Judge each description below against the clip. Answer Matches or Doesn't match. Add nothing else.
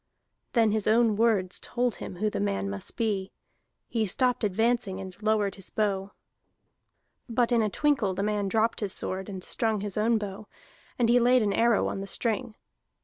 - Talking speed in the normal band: Matches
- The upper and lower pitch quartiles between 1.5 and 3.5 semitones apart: Matches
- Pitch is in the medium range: Doesn't match